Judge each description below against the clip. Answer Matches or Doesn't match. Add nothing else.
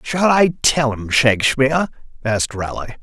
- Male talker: Matches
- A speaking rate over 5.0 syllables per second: Doesn't match